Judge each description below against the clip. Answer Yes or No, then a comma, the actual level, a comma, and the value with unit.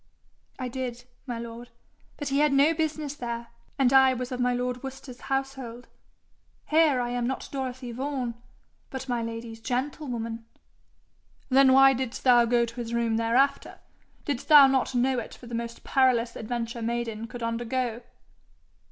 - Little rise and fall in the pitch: Yes, narrow, 2.3 semitones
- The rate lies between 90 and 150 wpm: No, average, 160 wpm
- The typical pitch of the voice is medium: No, high, 245 Hz